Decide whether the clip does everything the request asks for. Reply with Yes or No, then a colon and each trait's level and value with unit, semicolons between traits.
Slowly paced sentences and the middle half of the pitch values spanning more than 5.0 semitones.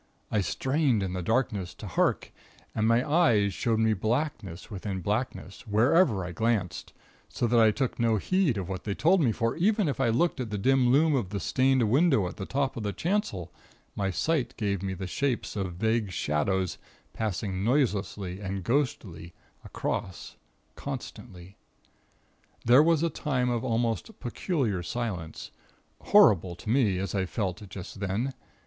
No: average, 165 wpm; wide, 5.5 semitones